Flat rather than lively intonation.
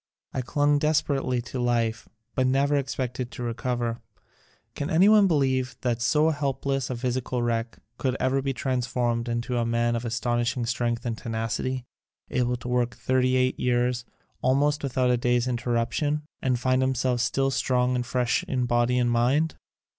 Yes: narrow, 1.8 semitones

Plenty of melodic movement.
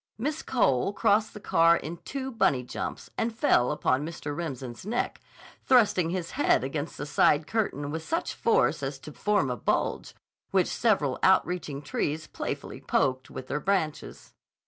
Yes: wide, 7.1 semitones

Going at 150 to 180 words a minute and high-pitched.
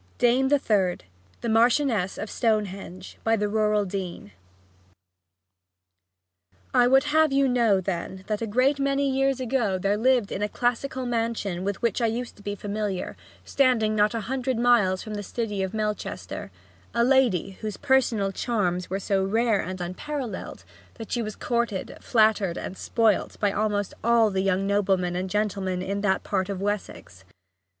Yes: average, 165 wpm; high, 215 Hz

